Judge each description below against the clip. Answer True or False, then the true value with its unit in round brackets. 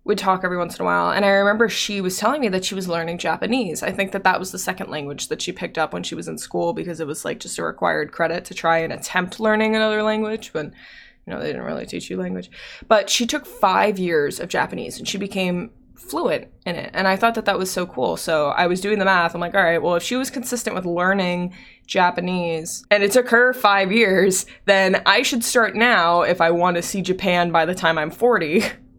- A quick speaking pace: True (250 wpm)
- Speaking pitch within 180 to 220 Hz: True (190 Hz)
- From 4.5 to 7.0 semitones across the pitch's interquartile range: False (4.0 semitones)